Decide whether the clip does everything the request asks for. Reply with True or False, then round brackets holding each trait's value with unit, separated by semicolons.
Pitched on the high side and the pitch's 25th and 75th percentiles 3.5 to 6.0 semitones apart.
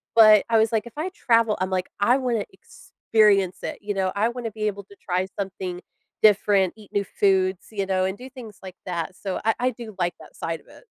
False (205 Hz; 3.0 semitones)